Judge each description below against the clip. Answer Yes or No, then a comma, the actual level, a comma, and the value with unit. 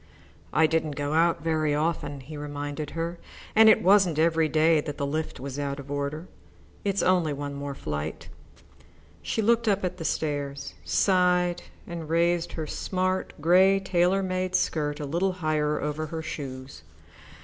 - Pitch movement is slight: No, average, 3.6 semitones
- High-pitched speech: No, medium, 160 Hz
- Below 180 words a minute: Yes, average, 160 wpm